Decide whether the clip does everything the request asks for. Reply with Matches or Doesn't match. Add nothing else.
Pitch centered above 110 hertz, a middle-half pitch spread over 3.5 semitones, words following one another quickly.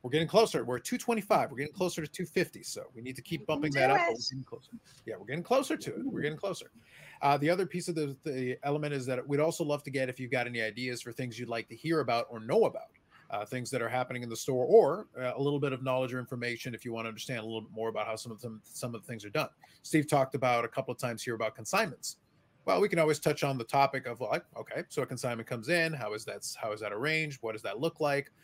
Matches